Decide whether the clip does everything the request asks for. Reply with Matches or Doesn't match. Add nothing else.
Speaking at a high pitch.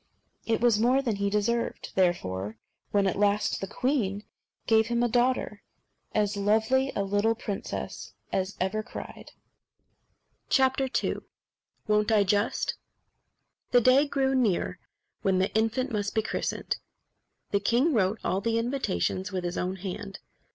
Matches